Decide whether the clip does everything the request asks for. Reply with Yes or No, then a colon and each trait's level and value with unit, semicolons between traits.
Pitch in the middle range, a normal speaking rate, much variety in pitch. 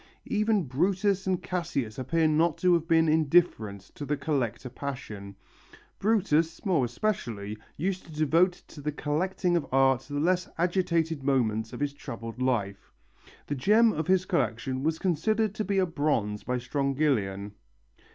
Yes: medium, 150 Hz; average, 150 wpm; wide, 5.9 semitones